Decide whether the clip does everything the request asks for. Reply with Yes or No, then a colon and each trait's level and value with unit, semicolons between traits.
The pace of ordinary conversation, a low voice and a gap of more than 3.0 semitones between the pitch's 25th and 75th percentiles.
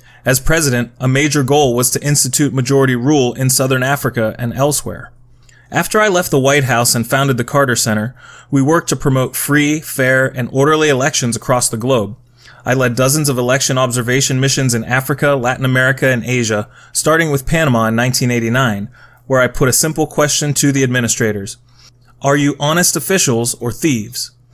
No: average, 175 wpm; low, 130 Hz; average, 2.7 semitones